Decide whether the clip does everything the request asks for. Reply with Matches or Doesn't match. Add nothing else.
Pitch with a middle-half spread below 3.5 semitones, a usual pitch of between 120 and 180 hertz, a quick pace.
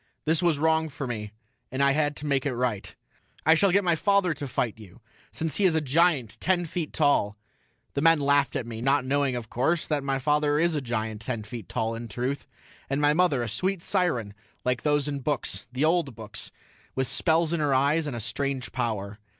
Doesn't match